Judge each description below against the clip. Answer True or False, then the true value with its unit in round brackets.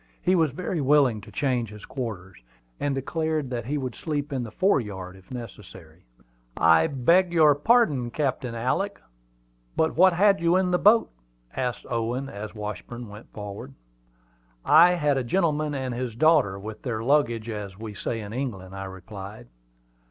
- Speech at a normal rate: True (165 wpm)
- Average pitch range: False (6.3 semitones)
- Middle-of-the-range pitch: False (125 Hz)